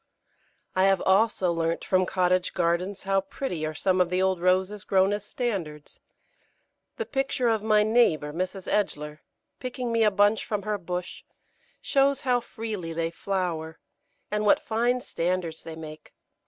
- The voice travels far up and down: No, average, 4.0 semitones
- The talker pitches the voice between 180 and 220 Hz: Yes, high, 190 Hz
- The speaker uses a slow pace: No, average, 155 wpm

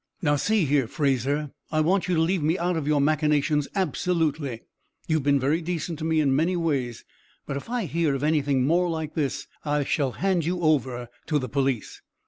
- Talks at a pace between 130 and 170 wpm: No, average, 200 wpm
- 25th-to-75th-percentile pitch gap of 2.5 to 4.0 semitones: Yes, average, 3.1 semitones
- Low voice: No, medium, 150 Hz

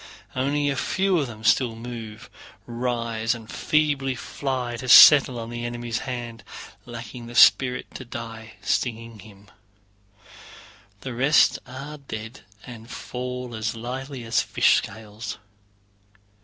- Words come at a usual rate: No, slow, 130 wpm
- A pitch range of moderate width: No, narrow, 2.3 semitones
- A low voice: Yes, low, 120 Hz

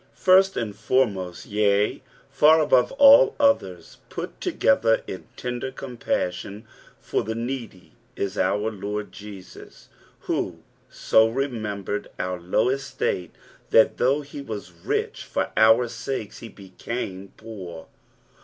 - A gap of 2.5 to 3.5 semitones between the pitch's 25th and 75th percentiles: No, average, 4.6 semitones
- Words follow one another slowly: Yes, slow, 120 wpm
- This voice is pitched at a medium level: No, low, 110 Hz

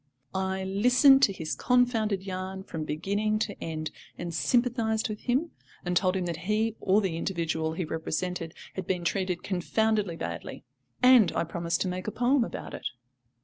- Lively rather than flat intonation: No, average, 4.3 semitones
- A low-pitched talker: No, high, 190 Hz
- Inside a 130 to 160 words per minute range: No, average, 170 wpm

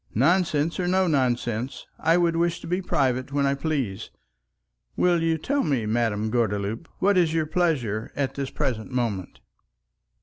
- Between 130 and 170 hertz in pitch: Yes, medium, 140 Hz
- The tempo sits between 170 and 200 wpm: No, average, 160 wpm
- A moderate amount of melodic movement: No, wide, 5.9 semitones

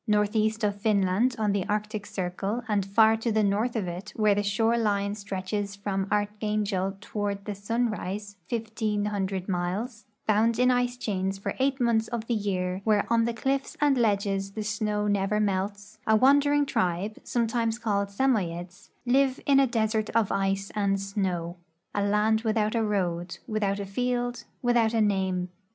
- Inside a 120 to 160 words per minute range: No, average, 170 wpm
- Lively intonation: No, narrow, 2.4 semitones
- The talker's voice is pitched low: No, high, 210 Hz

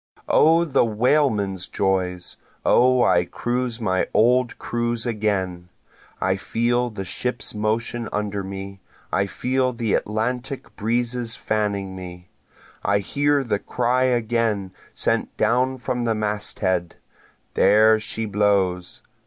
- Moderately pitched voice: No, low, 110 Hz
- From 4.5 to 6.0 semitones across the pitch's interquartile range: No, average, 3.8 semitones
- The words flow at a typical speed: No, slow, 120 wpm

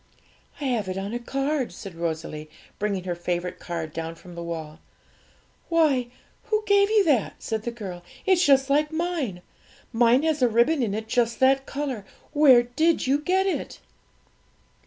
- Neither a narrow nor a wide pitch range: No, wide, 8.3 semitones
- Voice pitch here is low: No, high, 240 Hz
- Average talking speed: Yes, average, 170 wpm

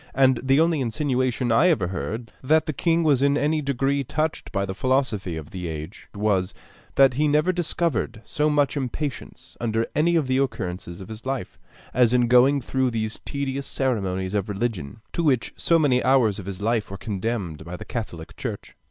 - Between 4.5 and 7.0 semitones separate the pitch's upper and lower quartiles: Yes, wide, 5.5 semitones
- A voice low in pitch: Yes, low, 125 Hz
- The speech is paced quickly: No, average, 190 wpm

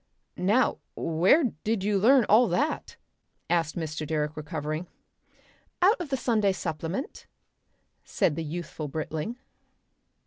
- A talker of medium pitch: Yes, medium, 175 Hz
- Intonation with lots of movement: Yes, wide, 6.8 semitones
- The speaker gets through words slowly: Yes, slow, 115 wpm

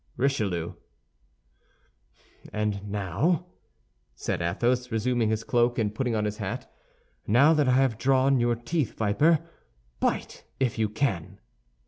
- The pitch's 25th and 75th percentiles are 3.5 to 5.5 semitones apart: Yes, average, 4.2 semitones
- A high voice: No, low, 120 Hz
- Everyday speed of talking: No, slow, 125 wpm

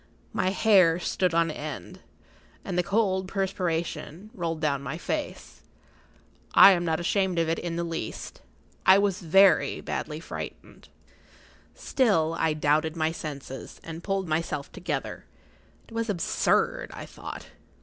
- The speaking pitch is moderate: Yes, medium, 170 Hz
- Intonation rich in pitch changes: No, average, 3.2 semitones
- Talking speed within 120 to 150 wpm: Yes, average, 140 wpm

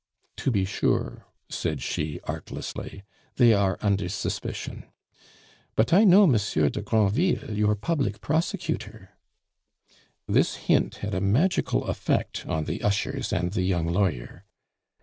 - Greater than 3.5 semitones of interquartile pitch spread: Yes, average, 5.2 semitones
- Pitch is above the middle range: No, low, 105 Hz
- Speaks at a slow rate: Yes, slow, 130 wpm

